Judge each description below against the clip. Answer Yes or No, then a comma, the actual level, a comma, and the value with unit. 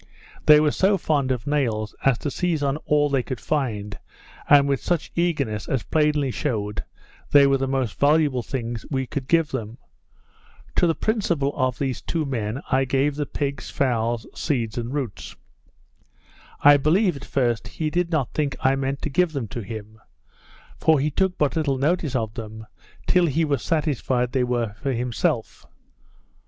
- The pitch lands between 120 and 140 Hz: Yes, low, 135 Hz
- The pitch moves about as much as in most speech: Yes, average, 3.8 semitones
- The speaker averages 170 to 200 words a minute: Yes, average, 175 wpm